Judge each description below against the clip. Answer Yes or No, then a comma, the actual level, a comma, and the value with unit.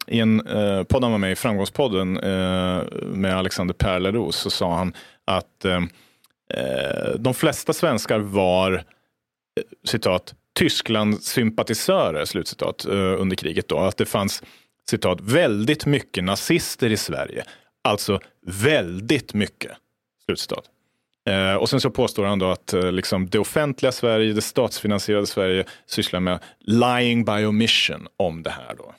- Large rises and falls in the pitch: No, average, 3.8 semitones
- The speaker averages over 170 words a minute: No, average, 140 wpm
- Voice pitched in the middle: No, low, 105 Hz